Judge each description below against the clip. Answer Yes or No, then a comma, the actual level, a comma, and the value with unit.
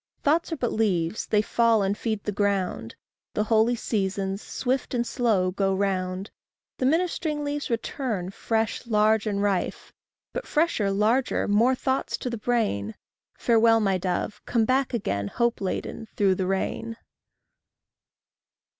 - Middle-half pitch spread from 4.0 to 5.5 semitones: No, average, 3.6 semitones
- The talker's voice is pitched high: Yes, high, 220 Hz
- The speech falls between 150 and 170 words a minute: No, average, 140 wpm